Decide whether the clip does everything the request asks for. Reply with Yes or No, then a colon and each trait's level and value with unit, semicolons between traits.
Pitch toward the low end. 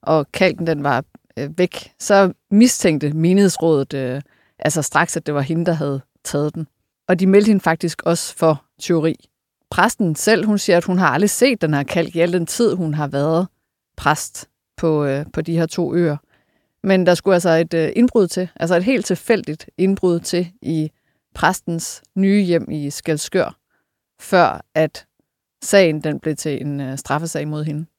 No: medium, 165 Hz